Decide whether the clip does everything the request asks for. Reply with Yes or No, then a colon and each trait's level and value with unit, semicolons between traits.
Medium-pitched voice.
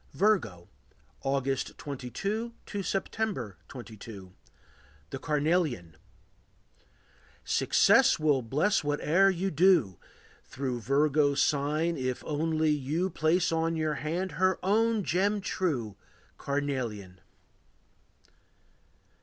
Yes: medium, 150 Hz